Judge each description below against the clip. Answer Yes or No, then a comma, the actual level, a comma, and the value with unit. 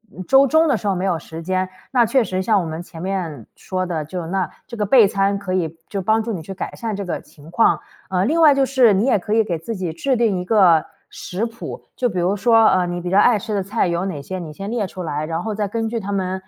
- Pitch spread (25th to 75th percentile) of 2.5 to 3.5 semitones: No, average, 4.1 semitones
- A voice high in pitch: Yes, high, 195 Hz